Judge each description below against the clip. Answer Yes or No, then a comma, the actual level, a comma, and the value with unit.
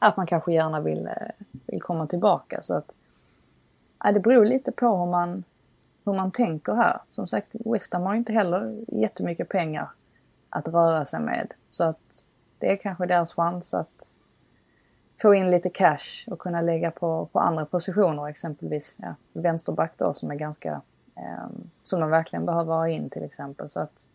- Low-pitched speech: No, medium, 175 Hz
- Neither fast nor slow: Yes, average, 175 wpm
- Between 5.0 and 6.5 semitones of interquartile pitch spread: No, average, 3.3 semitones